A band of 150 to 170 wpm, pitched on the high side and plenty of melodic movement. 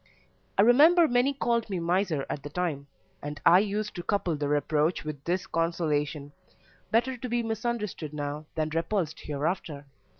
No: average, 160 wpm; medium, 170 Hz; wide, 6.7 semitones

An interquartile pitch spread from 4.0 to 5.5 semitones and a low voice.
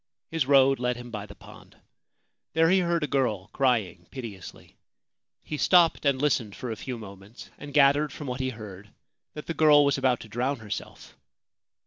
Yes: average, 4.8 semitones; low, 130 Hz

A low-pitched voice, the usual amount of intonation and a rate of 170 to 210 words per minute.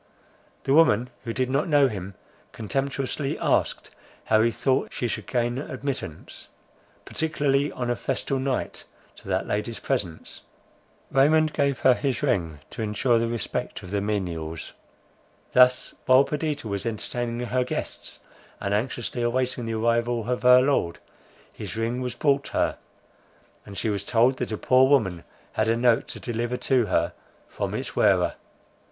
No: low, 120 Hz; average, 3.3 semitones; average, 155 wpm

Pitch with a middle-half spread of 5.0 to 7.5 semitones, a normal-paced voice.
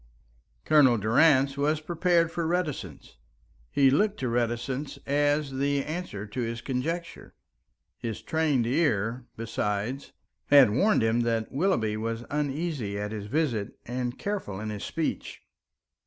No: average, 5.3 semitones; slow, 130 wpm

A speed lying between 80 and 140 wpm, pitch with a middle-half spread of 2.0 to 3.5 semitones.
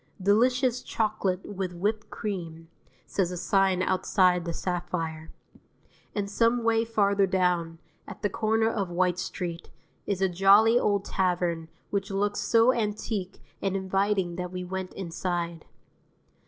Yes: slow, 135 wpm; average, 2.7 semitones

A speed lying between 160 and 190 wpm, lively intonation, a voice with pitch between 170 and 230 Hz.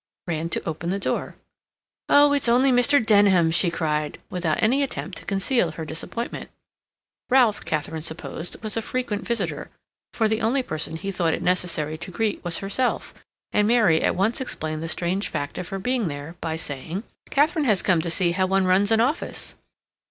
Yes: average, 185 wpm; wide, 5.8 semitones; high, 190 Hz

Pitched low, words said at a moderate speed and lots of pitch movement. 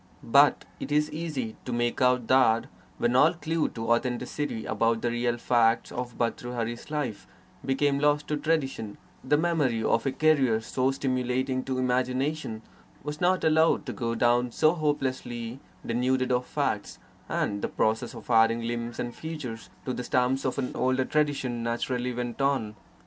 No: low, 125 Hz; average, 160 wpm; average, 3.2 semitones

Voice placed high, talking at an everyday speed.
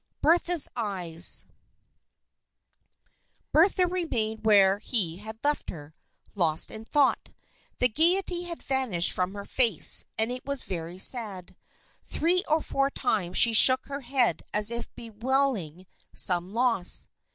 No: high, 230 Hz; slow, 130 wpm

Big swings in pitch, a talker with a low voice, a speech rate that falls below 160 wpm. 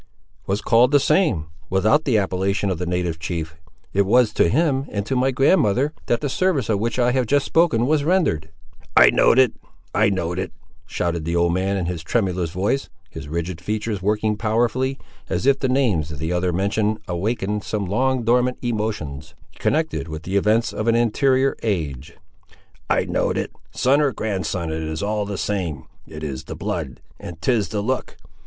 No: wide, 6.2 semitones; low, 105 Hz; average, 185 wpm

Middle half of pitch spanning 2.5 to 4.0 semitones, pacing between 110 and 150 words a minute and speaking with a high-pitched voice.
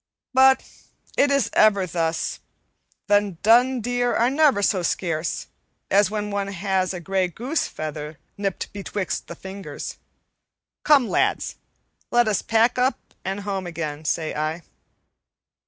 No: wide, 5.4 semitones; slow, 135 wpm; high, 200 Hz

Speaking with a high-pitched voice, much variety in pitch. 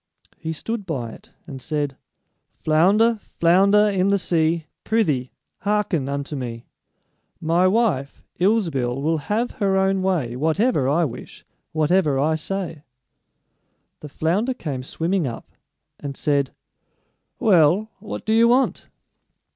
No: medium, 165 Hz; wide, 5.8 semitones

